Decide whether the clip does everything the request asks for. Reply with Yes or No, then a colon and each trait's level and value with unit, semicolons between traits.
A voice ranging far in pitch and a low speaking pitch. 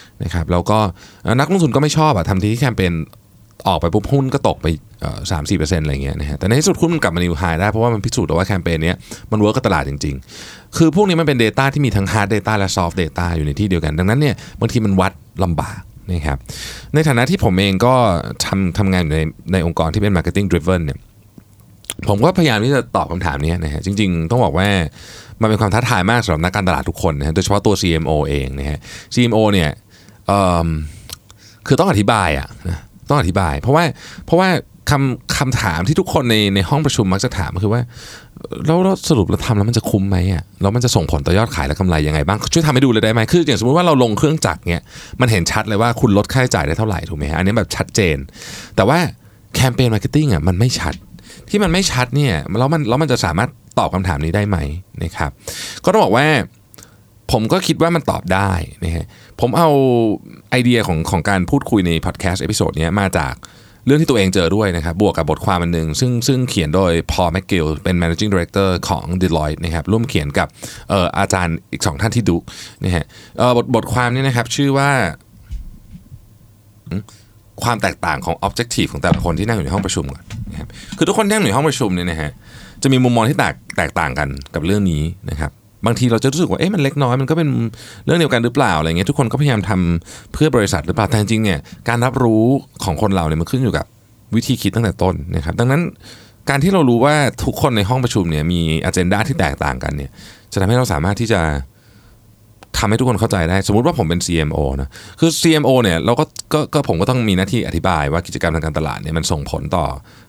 Yes: wide, 5.9 semitones; low, 100 Hz